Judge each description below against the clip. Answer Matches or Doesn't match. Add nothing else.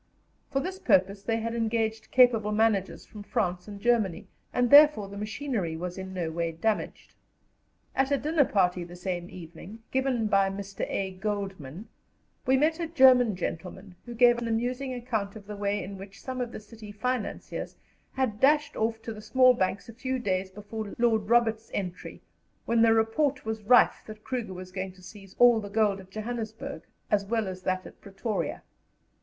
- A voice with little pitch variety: Doesn't match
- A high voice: Matches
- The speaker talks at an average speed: Matches